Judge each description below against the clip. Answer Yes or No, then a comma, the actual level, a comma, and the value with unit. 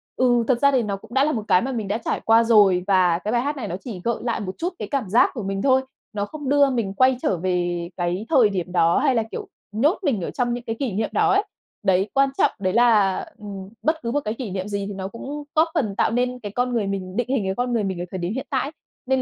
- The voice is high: Yes, high, 225 Hz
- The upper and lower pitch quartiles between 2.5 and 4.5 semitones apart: No, average, 4.9 semitones